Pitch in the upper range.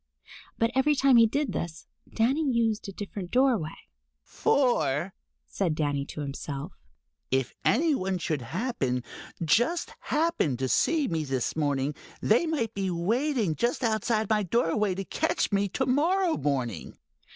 Yes: high, 205 Hz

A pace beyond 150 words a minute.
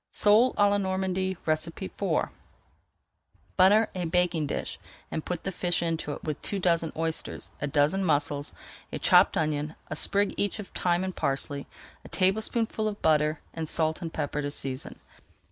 Yes: average, 160 wpm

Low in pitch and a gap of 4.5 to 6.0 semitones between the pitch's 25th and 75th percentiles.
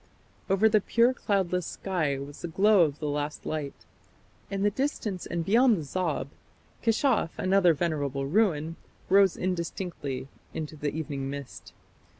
No: medium, 170 Hz; average, 5.1 semitones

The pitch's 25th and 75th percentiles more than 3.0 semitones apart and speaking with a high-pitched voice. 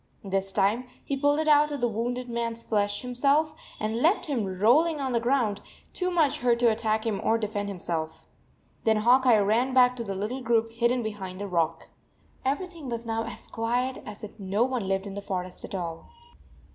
Yes: average, 3.9 semitones; high, 230 Hz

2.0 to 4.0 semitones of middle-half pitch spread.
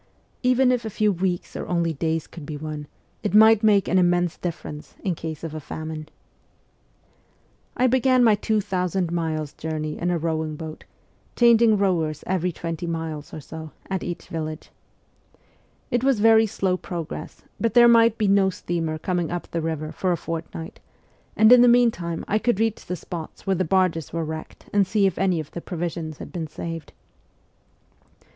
No: average, 4.6 semitones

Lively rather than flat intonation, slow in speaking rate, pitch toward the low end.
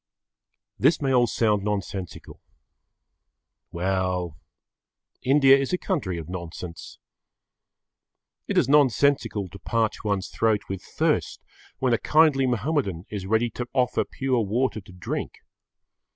Yes: wide, 5.8 semitones; slow, 125 wpm; low, 110 Hz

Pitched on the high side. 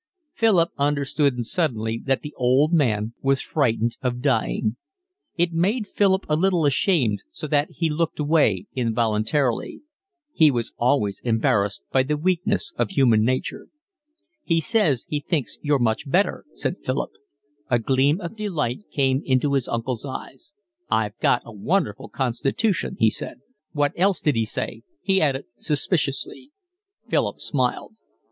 No: medium, 140 Hz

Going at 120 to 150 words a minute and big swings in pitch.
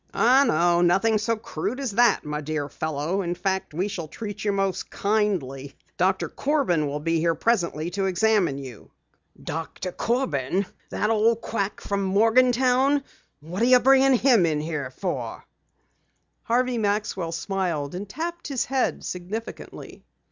Yes: average, 145 wpm; wide, 5.7 semitones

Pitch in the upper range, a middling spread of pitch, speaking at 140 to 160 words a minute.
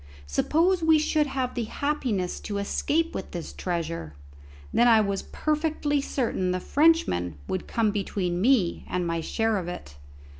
No: high, 215 Hz; wide, 8.6 semitones; average, 155 wpm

